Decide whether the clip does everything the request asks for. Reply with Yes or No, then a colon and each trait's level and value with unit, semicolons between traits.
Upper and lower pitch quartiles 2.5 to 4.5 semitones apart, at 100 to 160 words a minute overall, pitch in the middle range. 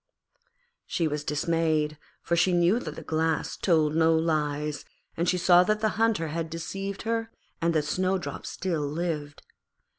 Yes: average, 3.0 semitones; average, 155 wpm; medium, 165 Hz